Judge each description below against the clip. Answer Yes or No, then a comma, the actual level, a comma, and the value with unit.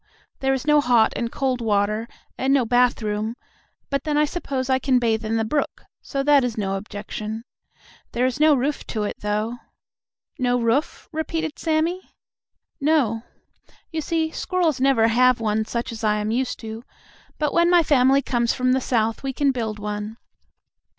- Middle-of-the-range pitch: No, very high, 250 Hz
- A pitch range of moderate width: Yes, average, 4.3 semitones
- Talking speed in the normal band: Yes, average, 175 wpm